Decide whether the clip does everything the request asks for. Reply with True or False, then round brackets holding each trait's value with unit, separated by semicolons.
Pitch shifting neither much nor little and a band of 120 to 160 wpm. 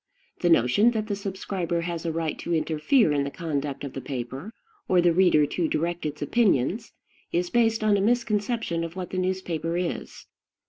False (4.5 semitones; 185 wpm)